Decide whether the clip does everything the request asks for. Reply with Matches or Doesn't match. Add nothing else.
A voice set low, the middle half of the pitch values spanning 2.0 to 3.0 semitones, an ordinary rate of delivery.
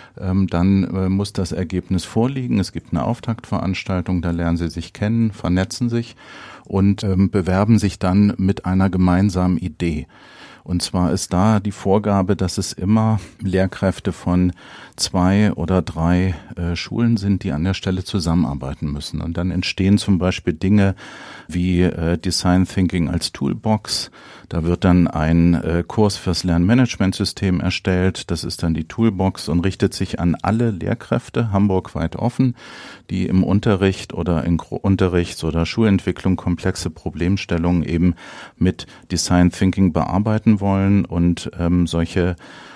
Matches